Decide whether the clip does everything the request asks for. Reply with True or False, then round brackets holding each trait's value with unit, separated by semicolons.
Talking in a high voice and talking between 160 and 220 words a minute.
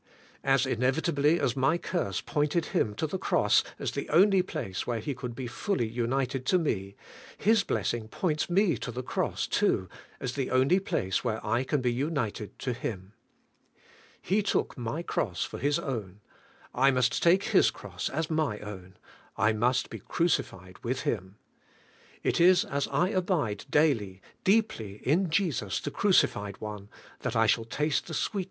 False (130 Hz; 175 wpm)